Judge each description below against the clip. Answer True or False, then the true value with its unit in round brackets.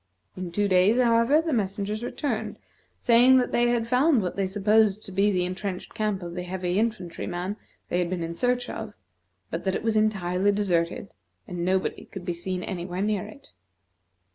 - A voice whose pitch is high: True (200 Hz)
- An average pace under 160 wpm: False (190 wpm)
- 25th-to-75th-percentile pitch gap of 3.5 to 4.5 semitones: True (3.8 semitones)